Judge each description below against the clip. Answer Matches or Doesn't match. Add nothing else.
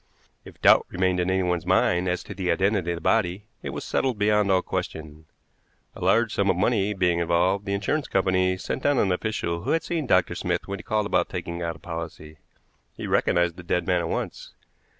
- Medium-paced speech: Doesn't match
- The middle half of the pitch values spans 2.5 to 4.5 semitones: Matches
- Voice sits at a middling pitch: Doesn't match